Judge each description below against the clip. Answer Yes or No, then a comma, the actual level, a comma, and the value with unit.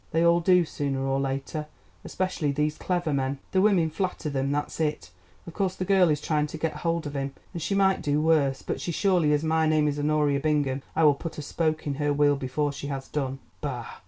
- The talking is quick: Yes, fast, 230 wpm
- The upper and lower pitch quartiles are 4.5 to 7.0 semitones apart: No, average, 2.8 semitones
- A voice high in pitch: No, medium, 150 Hz